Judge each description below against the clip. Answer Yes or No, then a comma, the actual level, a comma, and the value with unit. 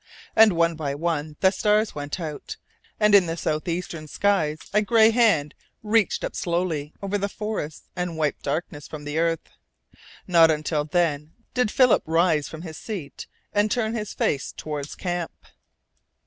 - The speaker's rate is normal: Yes, average, 160 wpm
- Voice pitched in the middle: Yes, medium, 170 Hz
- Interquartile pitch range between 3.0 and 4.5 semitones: No, average, 5.1 semitones